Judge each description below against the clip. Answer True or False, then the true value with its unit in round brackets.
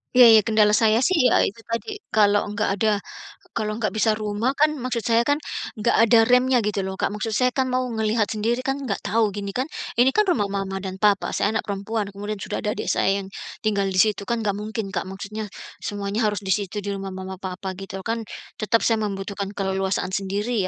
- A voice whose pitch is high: True (210 Hz)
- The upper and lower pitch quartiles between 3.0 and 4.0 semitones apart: False (2.6 semitones)